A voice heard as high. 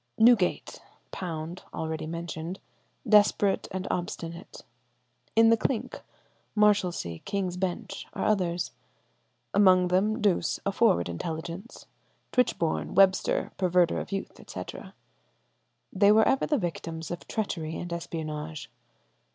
No: medium, 180 Hz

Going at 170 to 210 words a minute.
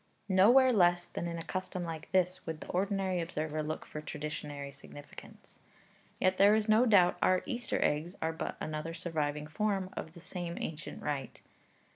Yes: average, 175 wpm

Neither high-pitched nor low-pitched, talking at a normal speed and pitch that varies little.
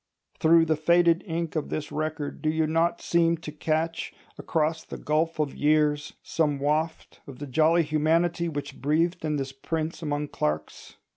Yes: medium, 155 Hz; average, 165 wpm; narrow, 1.8 semitones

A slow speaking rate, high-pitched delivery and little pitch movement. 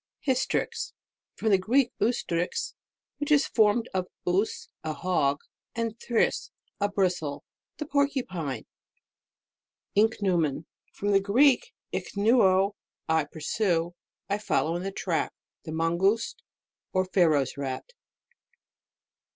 No: slow, 110 wpm; high, 195 Hz; average, 5.3 semitones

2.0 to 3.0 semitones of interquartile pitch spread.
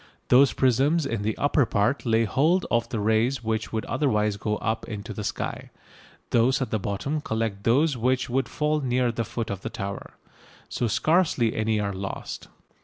No: average, 3.6 semitones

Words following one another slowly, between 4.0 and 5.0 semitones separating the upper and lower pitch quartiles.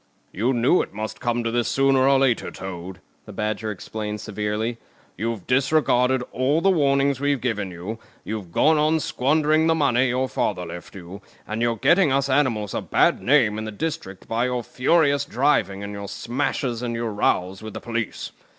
No: average, 185 wpm; average, 4.6 semitones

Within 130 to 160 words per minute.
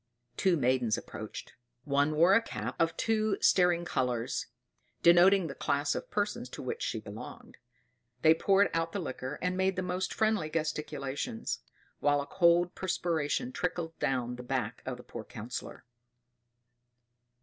Yes: average, 150 wpm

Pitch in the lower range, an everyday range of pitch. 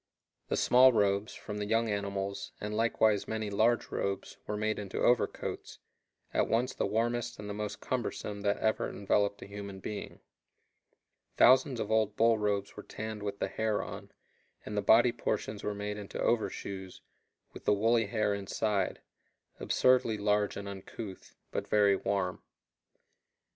No: low, 105 Hz; narrow, 1.7 semitones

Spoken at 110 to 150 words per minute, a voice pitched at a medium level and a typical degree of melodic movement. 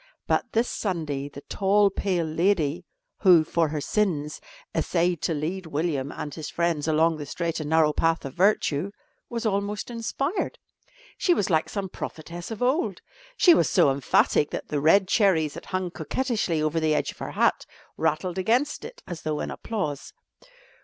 No: average, 175 wpm; medium, 170 Hz; average, 4.6 semitones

